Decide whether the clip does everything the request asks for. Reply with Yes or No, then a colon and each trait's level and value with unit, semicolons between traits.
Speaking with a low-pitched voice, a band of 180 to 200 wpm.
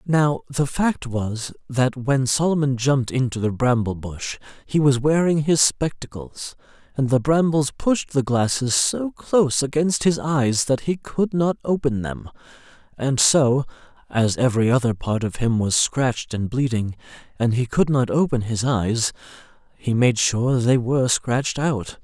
No: low, 130 Hz; average, 165 wpm